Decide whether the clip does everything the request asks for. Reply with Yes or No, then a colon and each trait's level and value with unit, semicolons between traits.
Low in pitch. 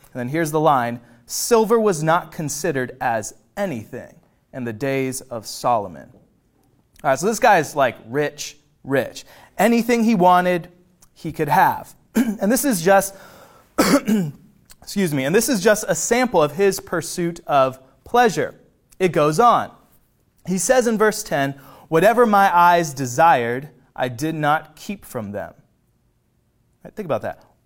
No: medium, 170 Hz